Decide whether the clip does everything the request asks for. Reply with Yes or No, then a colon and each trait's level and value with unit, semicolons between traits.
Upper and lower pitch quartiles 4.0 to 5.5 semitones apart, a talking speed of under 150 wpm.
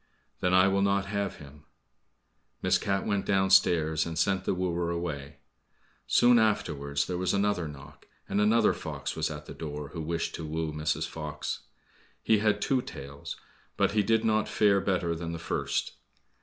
No: average, 4.4 semitones; average, 170 wpm